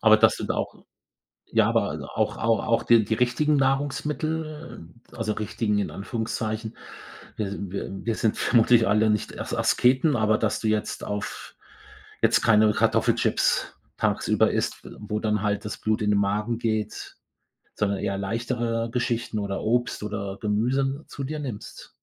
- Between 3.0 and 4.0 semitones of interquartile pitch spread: No, narrow, 2.6 semitones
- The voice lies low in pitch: Yes, low, 110 Hz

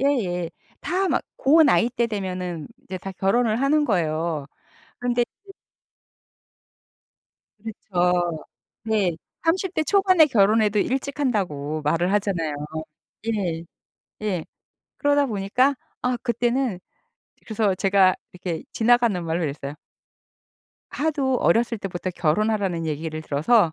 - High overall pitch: Yes, high, 205 Hz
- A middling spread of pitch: No, wide, 6.1 semitones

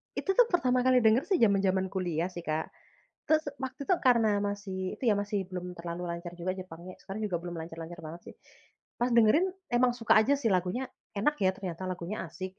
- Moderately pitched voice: No, high, 195 Hz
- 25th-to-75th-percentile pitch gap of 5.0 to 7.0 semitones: Yes, average, 5.3 semitones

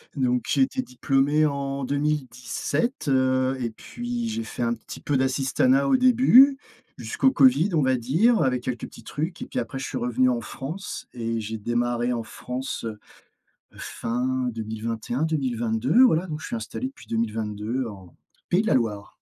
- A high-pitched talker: No, low, 130 Hz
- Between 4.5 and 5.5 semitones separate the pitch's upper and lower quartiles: Yes, average, 5.1 semitones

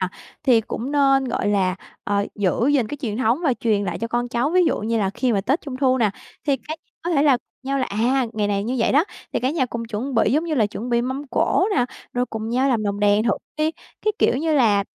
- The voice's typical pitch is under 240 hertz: No, high, 245 Hz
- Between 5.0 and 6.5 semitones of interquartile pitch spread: No, average, 4.3 semitones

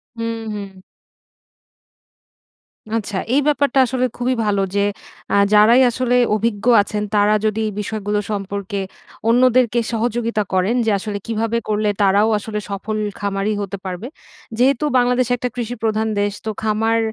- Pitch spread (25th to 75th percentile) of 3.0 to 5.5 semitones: No, narrow, 2.6 semitones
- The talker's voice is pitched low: No, high, 220 Hz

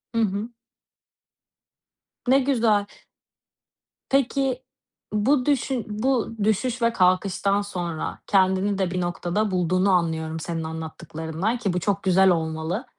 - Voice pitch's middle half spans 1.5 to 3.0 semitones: No, average, 4.7 semitones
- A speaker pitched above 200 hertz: No, high, 195 Hz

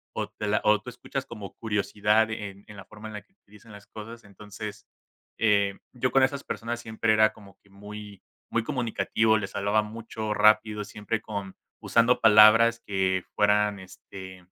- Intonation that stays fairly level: Yes, narrow, 1.6 semitones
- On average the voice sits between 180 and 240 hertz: No, low, 105 Hz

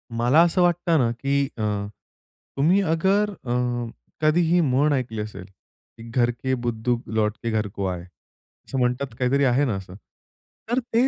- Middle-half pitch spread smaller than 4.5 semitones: No, wide, 5.5 semitones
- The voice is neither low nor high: No, low, 125 Hz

